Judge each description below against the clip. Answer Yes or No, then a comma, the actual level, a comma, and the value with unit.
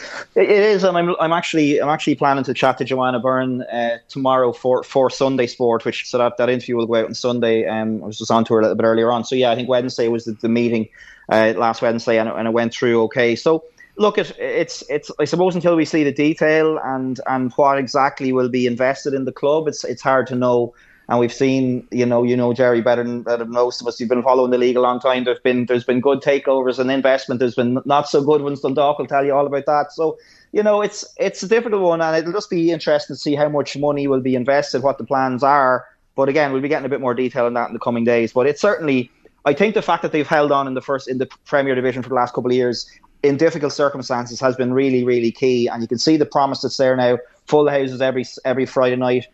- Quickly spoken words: Yes, fast, 265 wpm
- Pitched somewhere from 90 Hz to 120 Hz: No, low, 130 Hz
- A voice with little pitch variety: No, average, 3.0 semitones